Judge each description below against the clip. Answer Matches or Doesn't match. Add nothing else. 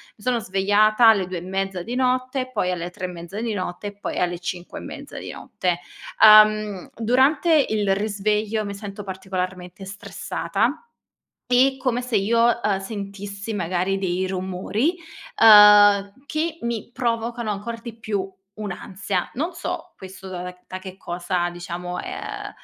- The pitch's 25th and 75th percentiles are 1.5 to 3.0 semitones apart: Doesn't match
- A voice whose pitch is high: Matches